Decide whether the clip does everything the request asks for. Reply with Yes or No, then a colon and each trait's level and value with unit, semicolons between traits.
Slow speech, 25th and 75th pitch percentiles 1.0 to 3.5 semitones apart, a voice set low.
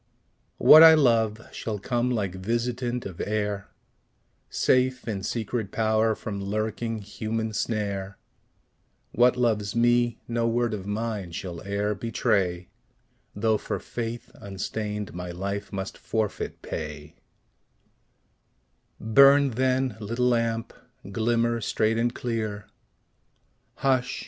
Yes: slow, 110 wpm; average, 2.8 semitones; low, 110 Hz